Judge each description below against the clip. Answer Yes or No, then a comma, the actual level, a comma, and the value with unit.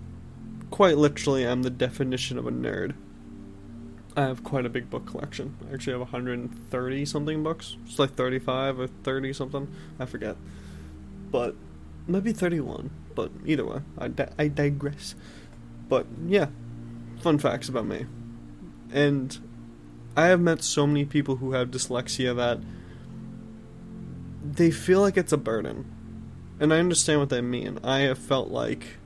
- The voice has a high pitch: No, low, 130 Hz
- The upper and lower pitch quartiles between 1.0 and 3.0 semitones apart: No, average, 3.7 semitones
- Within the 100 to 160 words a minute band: Yes, average, 150 wpm